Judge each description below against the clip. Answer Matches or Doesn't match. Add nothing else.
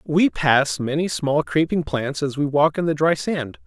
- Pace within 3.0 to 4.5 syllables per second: Matches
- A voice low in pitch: Doesn't match